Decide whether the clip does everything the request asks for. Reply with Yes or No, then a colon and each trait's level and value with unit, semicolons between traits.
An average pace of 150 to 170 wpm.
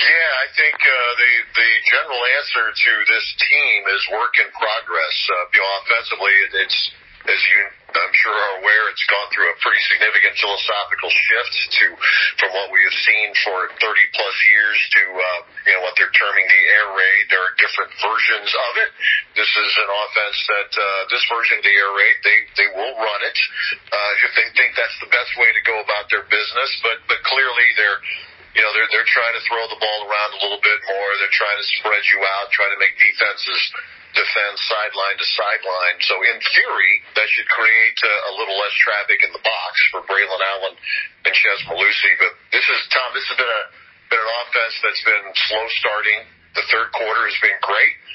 No: average, 200 wpm